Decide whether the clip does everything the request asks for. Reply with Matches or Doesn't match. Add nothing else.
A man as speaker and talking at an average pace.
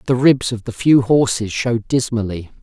Matches